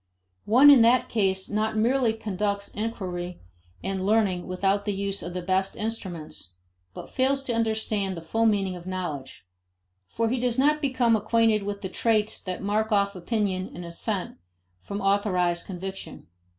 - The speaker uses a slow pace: No, average, 160 wpm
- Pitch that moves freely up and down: No, average, 3.3 semitones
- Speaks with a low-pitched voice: No, high, 200 Hz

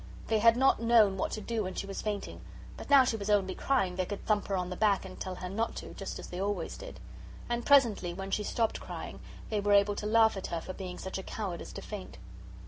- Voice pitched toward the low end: No, high, 205 Hz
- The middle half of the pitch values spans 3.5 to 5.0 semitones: No, average, 3.0 semitones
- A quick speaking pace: Yes, fast, 260 wpm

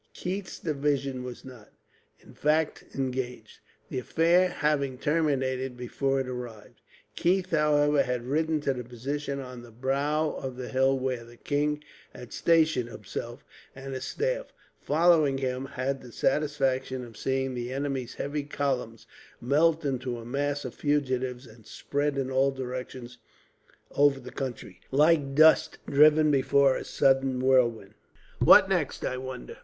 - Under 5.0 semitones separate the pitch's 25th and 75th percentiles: Yes, narrow, 2.6 semitones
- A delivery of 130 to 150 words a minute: Yes, average, 145 wpm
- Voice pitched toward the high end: No, low, 135 Hz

